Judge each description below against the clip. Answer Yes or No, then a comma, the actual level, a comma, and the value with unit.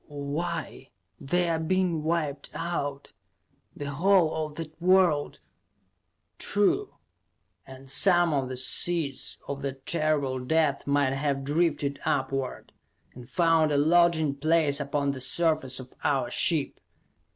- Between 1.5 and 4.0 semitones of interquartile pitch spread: Yes, average, 3.3 semitones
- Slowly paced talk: Yes, slow, 125 wpm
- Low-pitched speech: No, medium, 150 Hz